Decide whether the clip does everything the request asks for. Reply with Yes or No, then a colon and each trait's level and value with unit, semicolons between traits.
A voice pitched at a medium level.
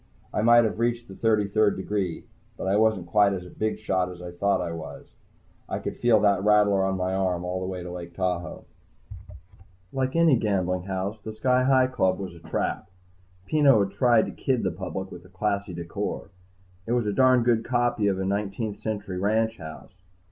No: low, 100 Hz